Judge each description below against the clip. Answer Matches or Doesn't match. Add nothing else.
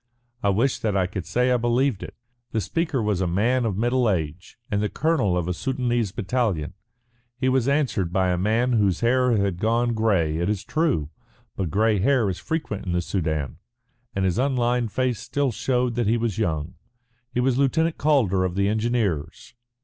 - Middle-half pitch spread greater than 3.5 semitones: Matches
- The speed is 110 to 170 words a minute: Doesn't match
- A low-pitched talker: Matches